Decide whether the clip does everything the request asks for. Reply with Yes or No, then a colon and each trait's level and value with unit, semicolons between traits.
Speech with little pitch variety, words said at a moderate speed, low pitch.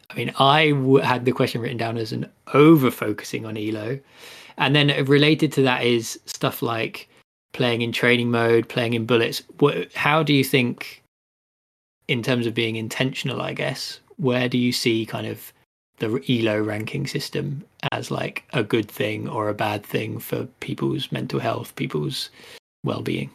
No: average, 3.4 semitones; average, 175 wpm; low, 125 Hz